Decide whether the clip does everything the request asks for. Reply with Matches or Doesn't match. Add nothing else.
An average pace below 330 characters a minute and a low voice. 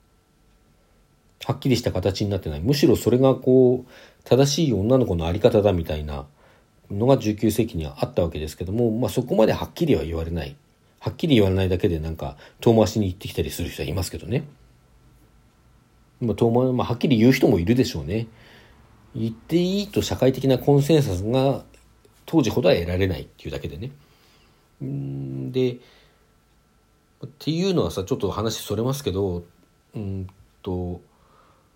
Doesn't match